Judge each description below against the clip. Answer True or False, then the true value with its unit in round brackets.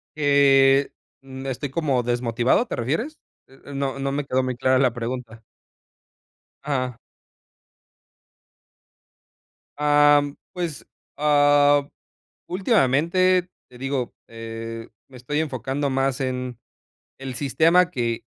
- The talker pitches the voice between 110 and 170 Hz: True (135 Hz)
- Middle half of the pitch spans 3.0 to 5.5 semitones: False (2.6 semitones)